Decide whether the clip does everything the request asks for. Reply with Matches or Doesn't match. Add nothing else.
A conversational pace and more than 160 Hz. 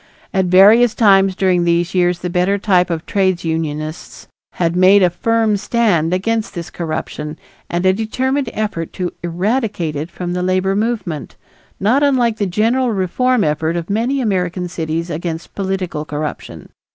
Matches